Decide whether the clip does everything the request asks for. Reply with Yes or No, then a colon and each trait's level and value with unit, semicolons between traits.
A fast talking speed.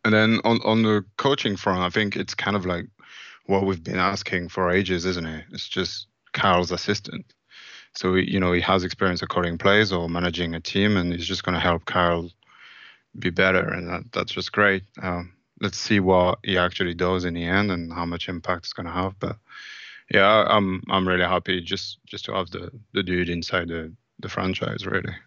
Yes: fast, 210 wpm